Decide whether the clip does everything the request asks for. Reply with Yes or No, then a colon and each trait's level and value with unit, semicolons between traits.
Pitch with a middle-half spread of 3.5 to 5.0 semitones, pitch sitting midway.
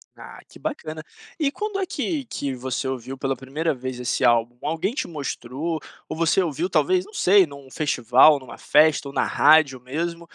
Yes: average, 4.7 semitones; medium, 150 Hz